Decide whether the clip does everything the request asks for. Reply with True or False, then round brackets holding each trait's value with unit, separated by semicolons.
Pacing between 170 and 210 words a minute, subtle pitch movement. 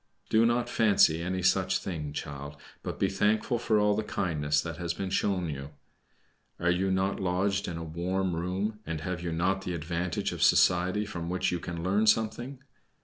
False (190 wpm; 3.3 semitones)